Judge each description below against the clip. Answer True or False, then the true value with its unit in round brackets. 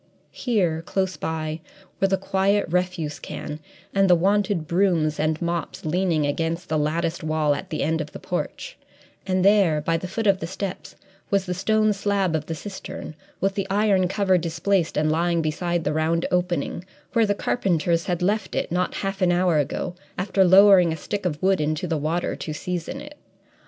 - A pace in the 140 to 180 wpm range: False (190 wpm)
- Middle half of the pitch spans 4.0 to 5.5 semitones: False (3.3 semitones)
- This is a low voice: False (180 Hz)